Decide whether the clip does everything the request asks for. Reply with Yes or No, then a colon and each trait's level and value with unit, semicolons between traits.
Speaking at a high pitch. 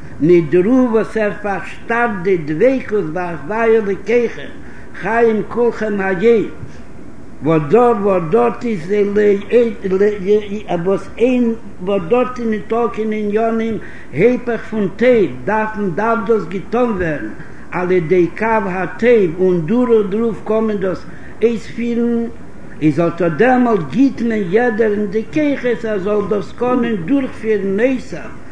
Yes: high, 215 Hz